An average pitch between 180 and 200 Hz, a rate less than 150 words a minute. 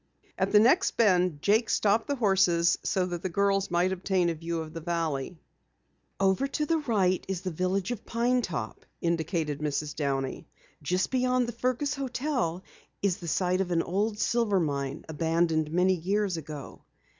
No: medium, 185 Hz; average, 170 wpm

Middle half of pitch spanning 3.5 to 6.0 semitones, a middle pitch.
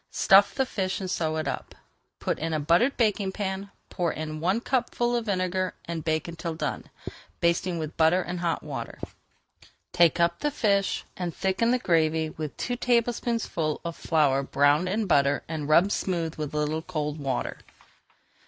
Yes: average, 3.9 semitones; medium, 170 Hz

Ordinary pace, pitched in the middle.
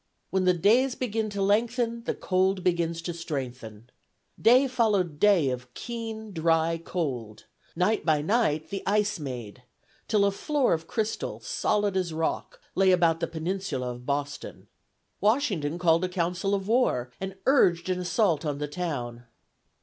Yes: average, 155 wpm; medium, 180 Hz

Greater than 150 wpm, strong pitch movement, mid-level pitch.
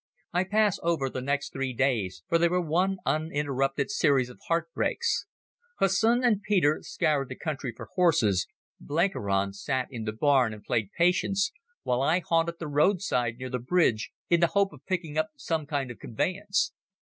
Yes: average, 175 wpm; wide, 5.8 semitones; medium, 150 Hz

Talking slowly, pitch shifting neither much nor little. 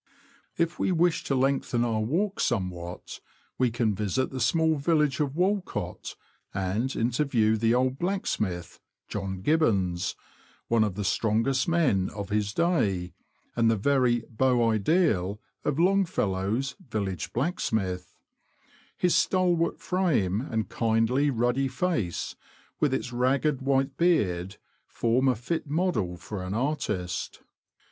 No: slow, 130 wpm; wide, 6.6 semitones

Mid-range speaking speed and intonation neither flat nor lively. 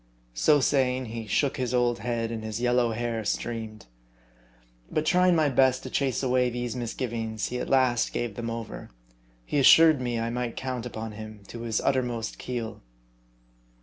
No: average, 170 wpm; narrow, 2.2 semitones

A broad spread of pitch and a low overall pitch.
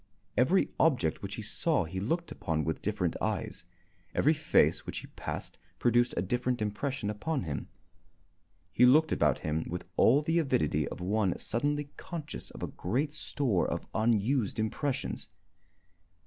Yes: wide, 7.5 semitones; low, 120 Hz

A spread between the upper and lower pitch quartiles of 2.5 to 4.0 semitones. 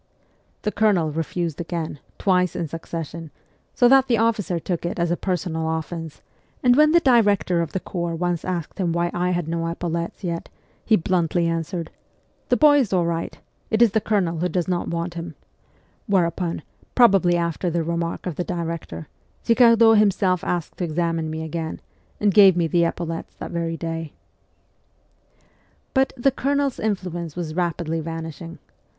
Yes: average, 2.9 semitones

